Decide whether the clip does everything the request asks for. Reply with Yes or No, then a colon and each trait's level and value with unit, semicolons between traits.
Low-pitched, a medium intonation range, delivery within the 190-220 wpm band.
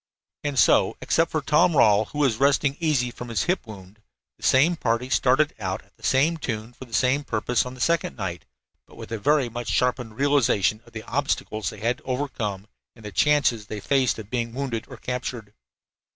Yes: low, 125 Hz; average, 4.4 semitones; fast, 205 wpm